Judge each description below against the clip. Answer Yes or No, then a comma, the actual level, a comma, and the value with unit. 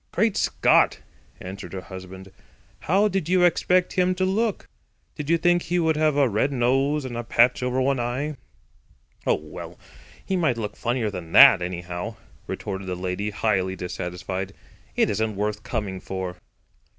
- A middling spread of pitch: No, wide, 8.6 semitones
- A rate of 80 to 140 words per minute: No, average, 165 wpm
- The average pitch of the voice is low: Yes, low, 120 Hz